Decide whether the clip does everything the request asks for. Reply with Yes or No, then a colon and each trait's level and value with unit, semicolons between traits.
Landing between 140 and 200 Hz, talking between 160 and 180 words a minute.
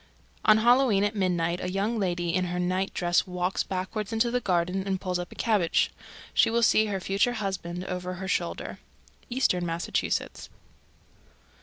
Yes: high, 190 Hz; average, 165 wpm